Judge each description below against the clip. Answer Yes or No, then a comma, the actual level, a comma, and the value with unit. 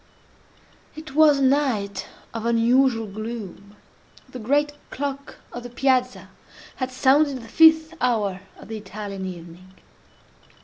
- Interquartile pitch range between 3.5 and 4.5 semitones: No, average, 4.9 semitones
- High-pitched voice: Yes, high, 245 Hz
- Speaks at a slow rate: Yes, slow, 125 wpm